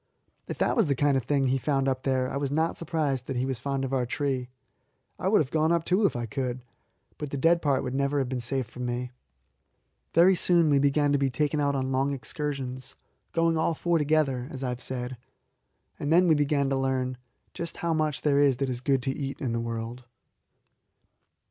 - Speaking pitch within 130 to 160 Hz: Yes, low, 135 Hz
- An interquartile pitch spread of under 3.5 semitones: Yes, average, 2.7 semitones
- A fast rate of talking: Yes, fast, 225 wpm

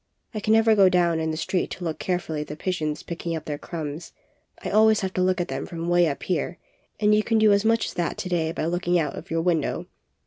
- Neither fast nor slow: No, fast, 255 wpm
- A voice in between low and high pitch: Yes, medium, 175 Hz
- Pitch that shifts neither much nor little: Yes, average, 3.2 semitones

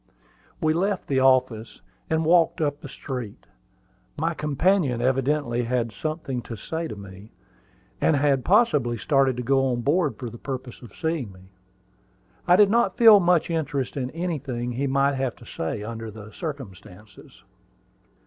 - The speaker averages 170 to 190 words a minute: No, average, 160 wpm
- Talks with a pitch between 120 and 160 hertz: Yes, low, 135 Hz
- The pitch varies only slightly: No, average, 5.0 semitones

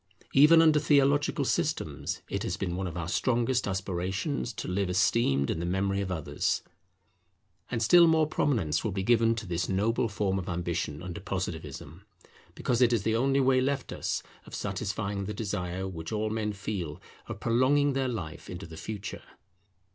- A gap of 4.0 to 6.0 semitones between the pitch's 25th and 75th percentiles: Yes, wide, 5.4 semitones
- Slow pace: No, average, 175 wpm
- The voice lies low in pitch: Yes, low, 100 Hz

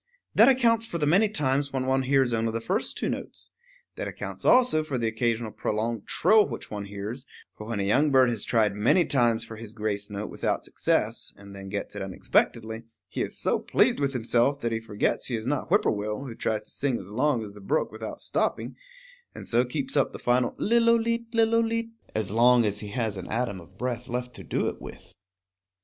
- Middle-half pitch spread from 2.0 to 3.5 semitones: No, average, 5.1 semitones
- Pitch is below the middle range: Yes, low, 120 Hz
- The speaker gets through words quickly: Yes, fast, 210 wpm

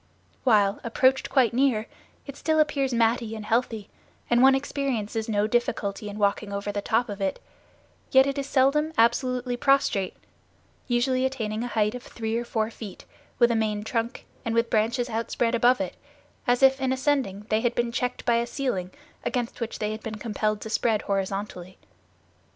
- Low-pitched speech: No, high, 230 Hz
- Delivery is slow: No, average, 180 wpm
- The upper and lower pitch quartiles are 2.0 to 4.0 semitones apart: Yes, average, 3.2 semitones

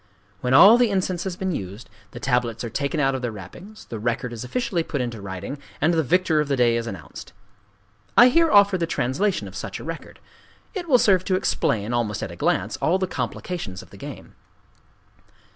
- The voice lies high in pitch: No, medium, 140 Hz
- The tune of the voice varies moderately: No, wide, 8.2 semitones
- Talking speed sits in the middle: No, fast, 210 wpm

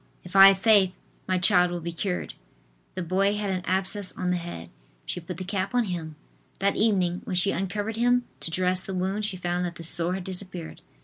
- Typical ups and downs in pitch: No, narrow, 1.8 semitones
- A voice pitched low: No, medium, 185 Hz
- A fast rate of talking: Yes, fast, 215 wpm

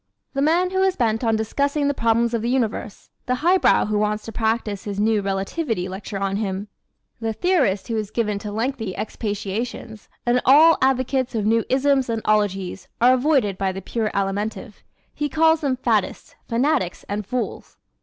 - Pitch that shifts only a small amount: No, average, 4.2 semitones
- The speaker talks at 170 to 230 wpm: Yes, average, 175 wpm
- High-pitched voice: Yes, high, 225 Hz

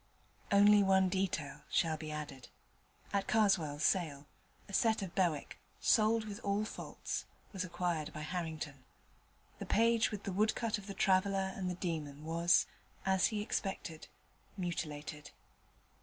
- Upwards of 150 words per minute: No, average, 140 wpm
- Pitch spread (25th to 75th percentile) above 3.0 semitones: Yes, average, 4.3 semitones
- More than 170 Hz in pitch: Yes, medium, 185 Hz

